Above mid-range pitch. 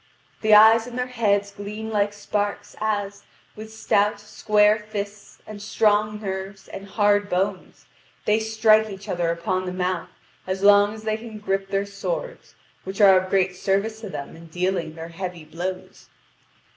Yes: high, 205 Hz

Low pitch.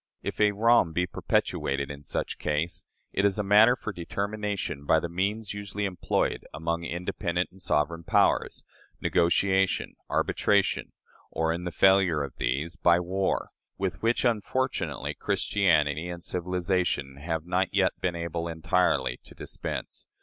Yes: very low, 90 Hz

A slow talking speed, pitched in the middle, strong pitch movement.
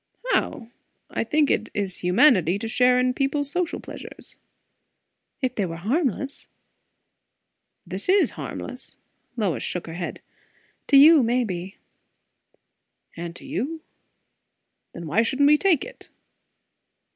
No: slow, 120 wpm; very high, 250 Hz; wide, 7.6 semitones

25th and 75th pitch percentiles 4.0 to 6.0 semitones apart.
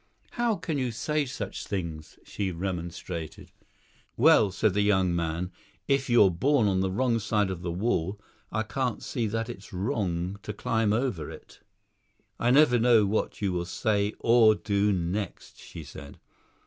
Yes: average, 4.5 semitones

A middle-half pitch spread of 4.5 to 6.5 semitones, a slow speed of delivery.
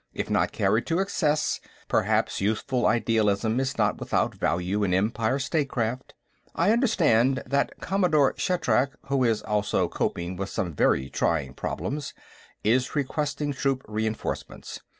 Yes: average, 5.2 semitones; slow, 130 wpm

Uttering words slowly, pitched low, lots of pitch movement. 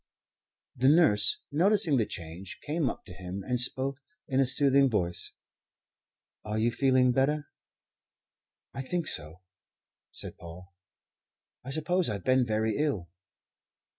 Yes: slow, 130 wpm; low, 130 Hz; wide, 6.2 semitones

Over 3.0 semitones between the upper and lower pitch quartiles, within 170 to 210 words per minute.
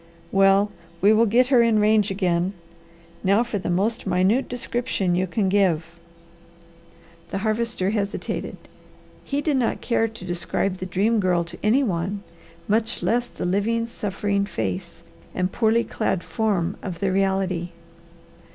No: average, 3.4 semitones; average, 145 wpm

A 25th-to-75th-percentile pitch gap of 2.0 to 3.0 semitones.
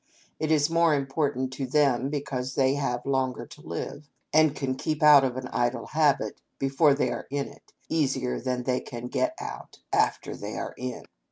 Yes: narrow, 2.6 semitones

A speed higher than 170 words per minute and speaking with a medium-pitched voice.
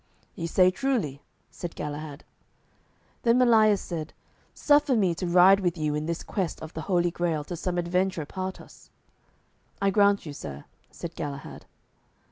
No: average, 155 wpm; medium, 175 Hz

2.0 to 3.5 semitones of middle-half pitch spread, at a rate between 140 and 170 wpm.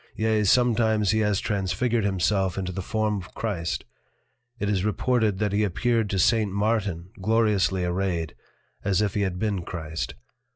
Yes: average, 2.7 semitones; average, 160 wpm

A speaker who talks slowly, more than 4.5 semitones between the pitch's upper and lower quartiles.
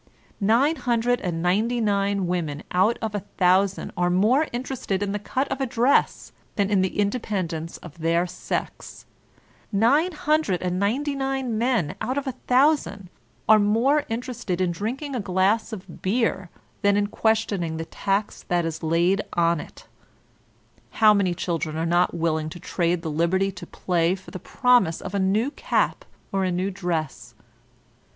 No: average, 165 wpm; average, 4.9 semitones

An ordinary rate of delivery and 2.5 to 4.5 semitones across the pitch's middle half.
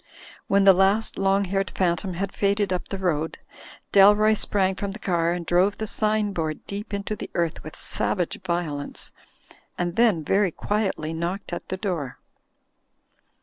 Yes: average, 160 wpm; average, 2.8 semitones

